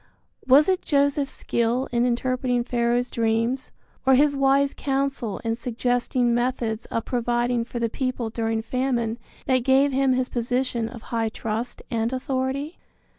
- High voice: Yes, high, 245 Hz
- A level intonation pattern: Yes, narrow, 2.2 semitones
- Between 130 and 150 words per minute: Yes, average, 145 wpm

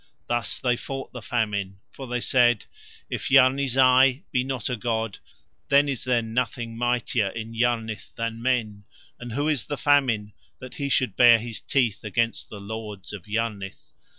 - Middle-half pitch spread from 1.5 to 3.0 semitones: Yes, narrow, 2.6 semitones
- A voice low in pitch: Yes, low, 120 Hz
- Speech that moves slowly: No, average, 170 wpm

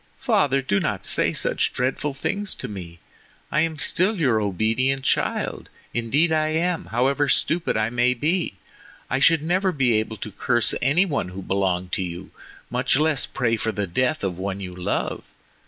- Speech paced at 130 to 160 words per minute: No, average, 175 wpm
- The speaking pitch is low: Yes, low, 125 Hz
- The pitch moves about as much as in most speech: No, wide, 7.3 semitones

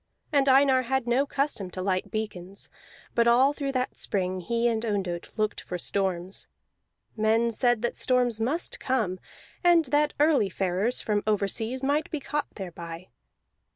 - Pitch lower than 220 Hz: No, high, 230 Hz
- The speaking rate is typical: Yes, average, 155 wpm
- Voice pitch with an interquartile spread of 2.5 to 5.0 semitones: No, wide, 5.5 semitones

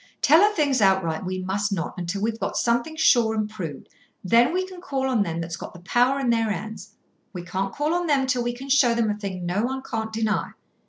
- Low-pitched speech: No, high, 225 Hz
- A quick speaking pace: Yes, fast, 235 wpm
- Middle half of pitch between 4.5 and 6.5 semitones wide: Yes, wide, 5.6 semitones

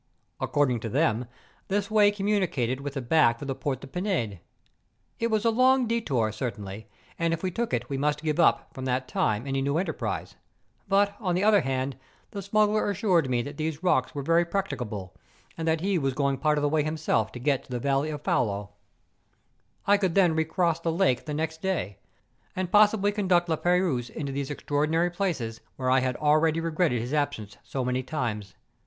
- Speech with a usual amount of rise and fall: No, wide, 6.1 semitones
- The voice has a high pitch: No, medium, 150 Hz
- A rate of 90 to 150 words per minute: No, average, 200 wpm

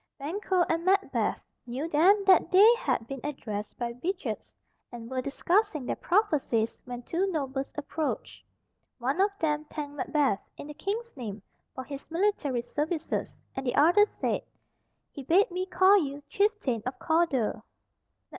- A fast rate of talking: No, average, 150 wpm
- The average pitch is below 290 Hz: No, very high, 300 Hz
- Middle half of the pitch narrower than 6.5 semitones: Yes, wide, 6.1 semitones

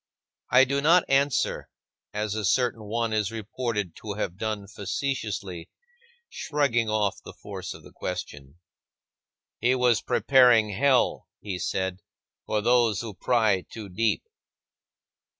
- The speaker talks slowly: Yes, slow, 130 wpm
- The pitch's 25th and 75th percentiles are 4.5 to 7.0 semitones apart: No, average, 3.5 semitones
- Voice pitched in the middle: No, low, 110 Hz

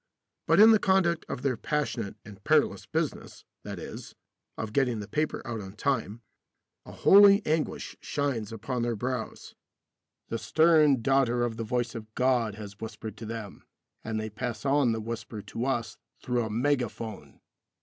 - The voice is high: No, low, 120 Hz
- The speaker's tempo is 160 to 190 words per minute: Yes, average, 170 wpm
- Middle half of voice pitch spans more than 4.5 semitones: No, average, 3.9 semitones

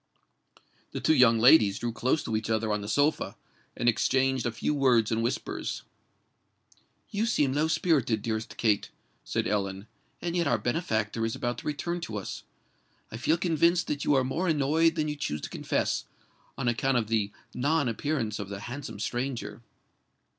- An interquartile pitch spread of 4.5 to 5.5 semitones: Yes, average, 5.2 semitones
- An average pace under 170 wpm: No, average, 175 wpm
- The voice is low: Yes, low, 125 Hz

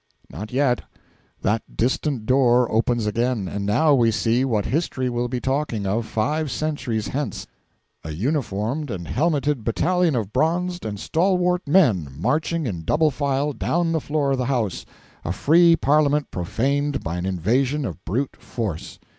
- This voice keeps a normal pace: Yes, average, 155 wpm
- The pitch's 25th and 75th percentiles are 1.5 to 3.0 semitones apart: No, wide, 5.6 semitones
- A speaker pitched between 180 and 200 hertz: No, low, 130 Hz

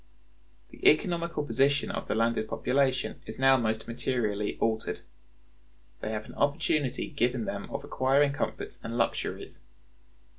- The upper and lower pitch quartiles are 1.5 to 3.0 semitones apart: No, average, 4.1 semitones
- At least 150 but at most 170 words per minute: No, slow, 135 wpm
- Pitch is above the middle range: No, low, 130 Hz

